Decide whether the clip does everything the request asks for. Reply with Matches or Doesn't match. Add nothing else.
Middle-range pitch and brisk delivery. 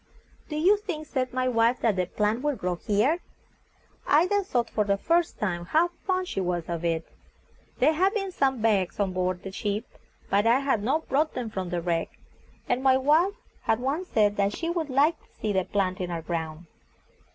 Doesn't match